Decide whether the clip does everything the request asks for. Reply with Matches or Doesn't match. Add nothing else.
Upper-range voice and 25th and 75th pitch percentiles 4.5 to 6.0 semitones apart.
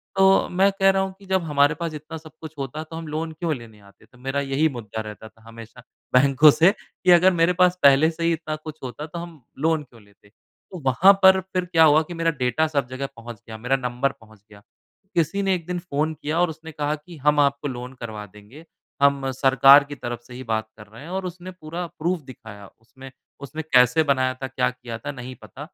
Doesn't match